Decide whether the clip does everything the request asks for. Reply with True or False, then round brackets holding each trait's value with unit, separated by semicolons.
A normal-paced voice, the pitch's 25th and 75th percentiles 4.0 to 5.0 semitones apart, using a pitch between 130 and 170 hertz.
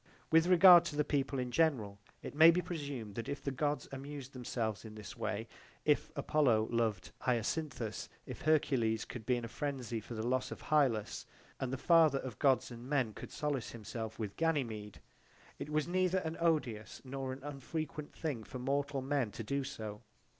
True (190 wpm; 4.6 semitones; 135 Hz)